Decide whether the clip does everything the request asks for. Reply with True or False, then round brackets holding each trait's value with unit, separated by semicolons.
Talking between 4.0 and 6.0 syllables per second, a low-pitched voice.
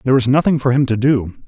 False (7.0 syllables/s; 130 Hz)